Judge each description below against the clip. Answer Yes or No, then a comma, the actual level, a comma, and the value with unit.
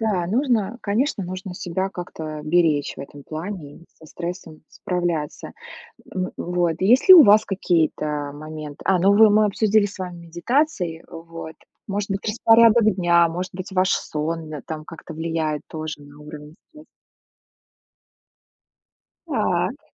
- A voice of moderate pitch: Yes, medium, 175 Hz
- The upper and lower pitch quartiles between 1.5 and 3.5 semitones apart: No, average, 4.4 semitones